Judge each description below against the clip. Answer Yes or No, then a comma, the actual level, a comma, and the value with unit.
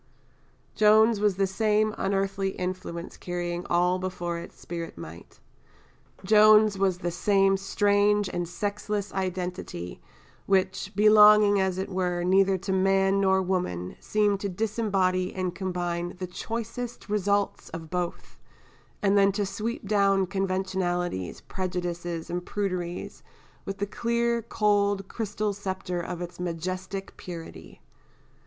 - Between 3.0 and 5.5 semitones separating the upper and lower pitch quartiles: No, narrow, 2.4 semitones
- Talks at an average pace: No, slow, 125 wpm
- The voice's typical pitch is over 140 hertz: Yes, high, 190 Hz